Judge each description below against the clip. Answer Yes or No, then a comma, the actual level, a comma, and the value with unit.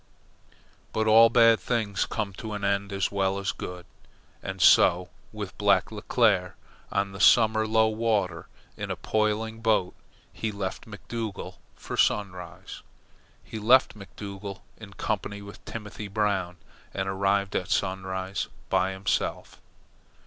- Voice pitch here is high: No, low, 100 Hz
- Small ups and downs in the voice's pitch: Yes, narrow, 2.2 semitones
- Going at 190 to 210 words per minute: No, slow, 135 wpm